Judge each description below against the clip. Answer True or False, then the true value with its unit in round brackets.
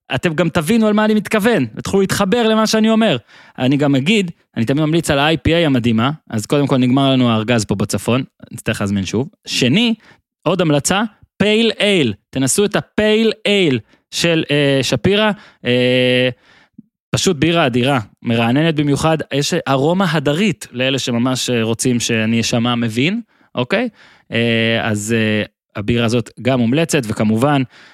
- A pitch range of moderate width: False (8.3 semitones)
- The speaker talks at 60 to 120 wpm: False (145 wpm)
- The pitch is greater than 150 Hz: False (140 Hz)